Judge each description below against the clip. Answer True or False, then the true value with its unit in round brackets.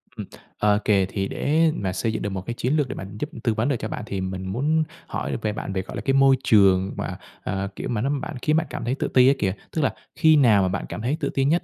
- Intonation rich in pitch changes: True (6.4 semitones)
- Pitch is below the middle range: True (120 Hz)